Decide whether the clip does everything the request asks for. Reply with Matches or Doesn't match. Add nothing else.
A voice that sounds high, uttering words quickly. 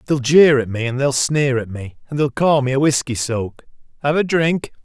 Doesn't match